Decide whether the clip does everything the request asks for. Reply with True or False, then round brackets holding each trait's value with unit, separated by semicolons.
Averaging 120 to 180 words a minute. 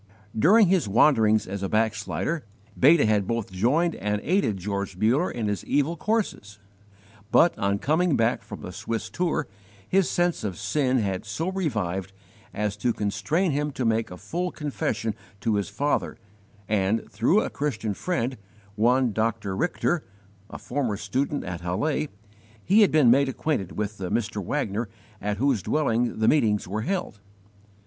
True (160 wpm)